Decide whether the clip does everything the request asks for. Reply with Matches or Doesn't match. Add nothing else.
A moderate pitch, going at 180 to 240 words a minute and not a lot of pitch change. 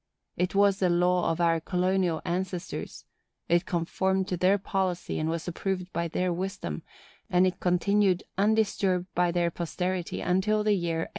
Doesn't match